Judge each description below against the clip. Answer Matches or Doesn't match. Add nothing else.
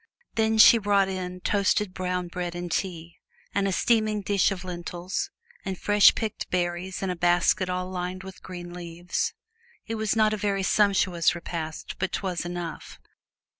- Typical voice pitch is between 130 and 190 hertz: Matches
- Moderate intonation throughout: Doesn't match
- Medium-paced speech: Matches